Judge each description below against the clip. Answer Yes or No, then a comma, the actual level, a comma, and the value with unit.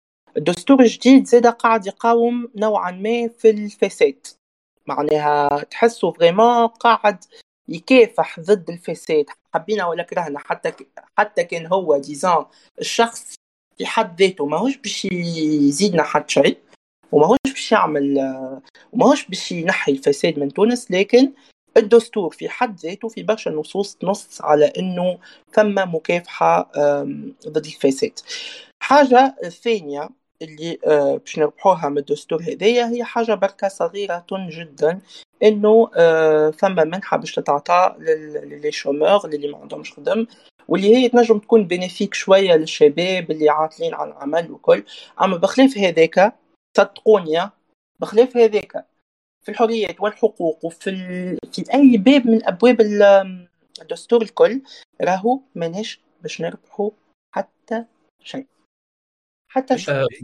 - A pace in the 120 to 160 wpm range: Yes, average, 125 wpm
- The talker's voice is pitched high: Yes, high, 205 Hz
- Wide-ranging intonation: Yes, wide, 6.1 semitones